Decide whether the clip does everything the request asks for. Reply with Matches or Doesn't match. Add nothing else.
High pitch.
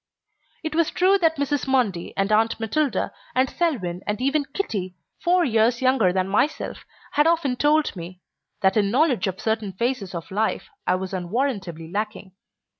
Matches